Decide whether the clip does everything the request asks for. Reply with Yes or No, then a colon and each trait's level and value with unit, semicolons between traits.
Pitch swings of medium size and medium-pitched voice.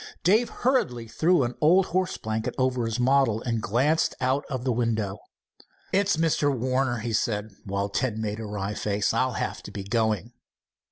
No: average, 4.3 semitones; low, 120 Hz